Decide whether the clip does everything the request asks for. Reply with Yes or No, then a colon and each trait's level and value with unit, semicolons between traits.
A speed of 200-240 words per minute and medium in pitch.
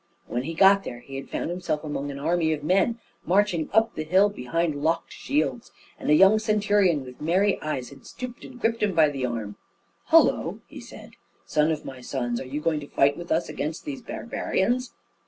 Yes: fast, 205 wpm; medium, 165 Hz